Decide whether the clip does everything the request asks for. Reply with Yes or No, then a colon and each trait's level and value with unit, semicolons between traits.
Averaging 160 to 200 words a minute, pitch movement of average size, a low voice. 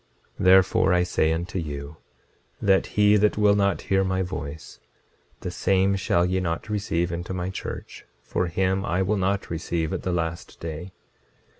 No: average, 170 wpm; narrow, 2.3 semitones; very low, 90 Hz